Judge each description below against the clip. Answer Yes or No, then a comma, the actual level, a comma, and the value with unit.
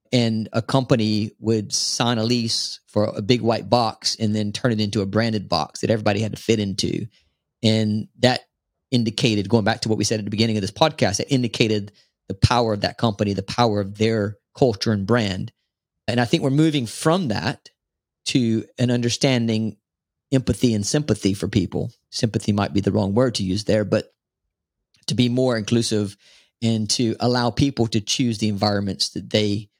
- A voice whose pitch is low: Yes, low, 110 Hz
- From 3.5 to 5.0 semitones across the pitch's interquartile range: No, narrow, 2.5 semitones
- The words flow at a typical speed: Yes, average, 190 wpm